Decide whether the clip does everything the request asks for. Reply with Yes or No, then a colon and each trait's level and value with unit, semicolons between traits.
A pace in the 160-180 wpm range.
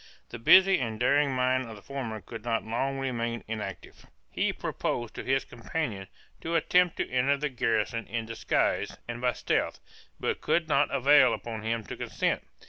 Yes: average, 175 wpm